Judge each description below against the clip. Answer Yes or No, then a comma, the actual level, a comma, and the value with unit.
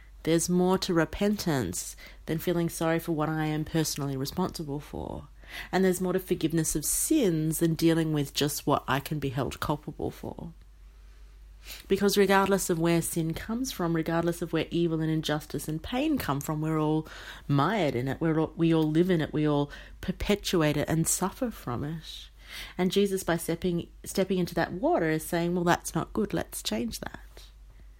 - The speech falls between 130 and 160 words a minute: No, average, 185 wpm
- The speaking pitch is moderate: Yes, medium, 165 Hz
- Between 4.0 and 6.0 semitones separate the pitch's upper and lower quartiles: No, average, 3.2 semitones